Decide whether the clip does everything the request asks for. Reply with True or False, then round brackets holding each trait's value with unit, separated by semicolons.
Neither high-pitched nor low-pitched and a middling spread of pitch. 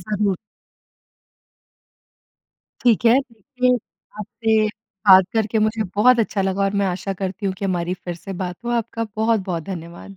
False (205 Hz; 3.1 semitones)